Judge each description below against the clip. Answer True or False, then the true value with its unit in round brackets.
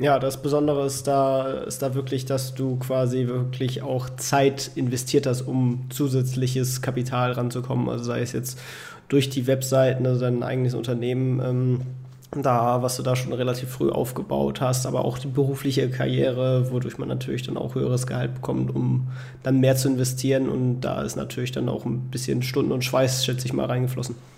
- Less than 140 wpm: False (185 wpm)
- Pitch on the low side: True (130 Hz)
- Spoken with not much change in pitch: True (1.1 semitones)